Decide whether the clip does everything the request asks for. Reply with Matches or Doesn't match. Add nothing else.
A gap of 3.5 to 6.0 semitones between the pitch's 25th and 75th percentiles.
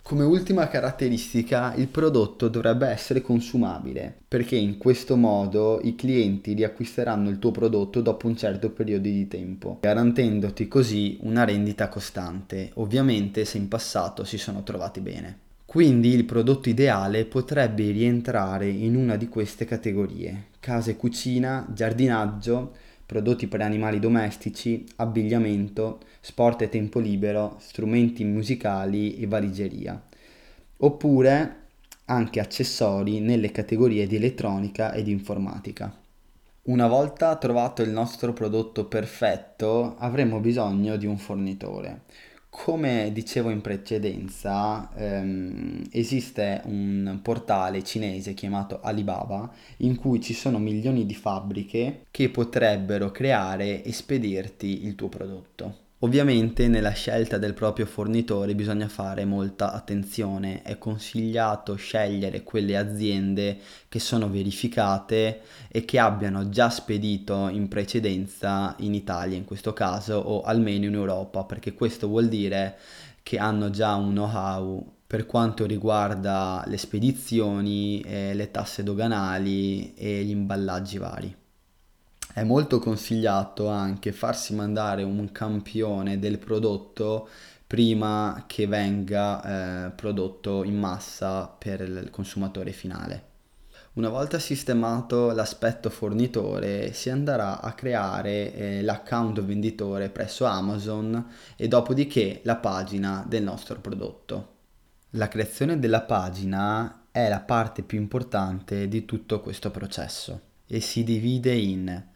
Doesn't match